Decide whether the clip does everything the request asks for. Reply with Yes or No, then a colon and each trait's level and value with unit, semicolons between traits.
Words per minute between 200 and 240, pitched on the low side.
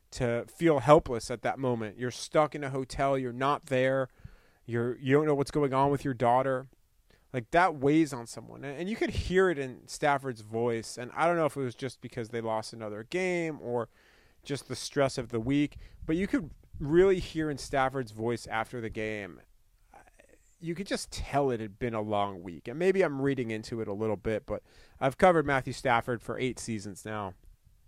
Yes: fast, 205 wpm; low, 130 Hz